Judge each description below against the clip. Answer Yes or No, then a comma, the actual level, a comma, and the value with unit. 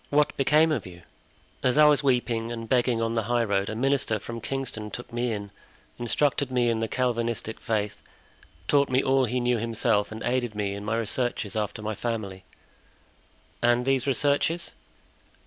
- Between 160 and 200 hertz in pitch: No, low, 120 Hz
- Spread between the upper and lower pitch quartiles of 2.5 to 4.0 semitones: Yes, average, 2.9 semitones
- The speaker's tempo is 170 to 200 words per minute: Yes, average, 175 wpm